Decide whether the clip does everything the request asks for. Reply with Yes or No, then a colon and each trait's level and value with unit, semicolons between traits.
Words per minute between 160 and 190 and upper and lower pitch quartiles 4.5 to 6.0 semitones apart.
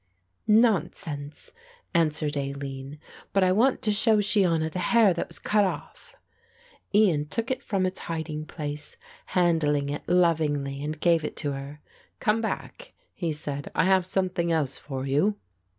No: average, 150 wpm; average, 4.8 semitones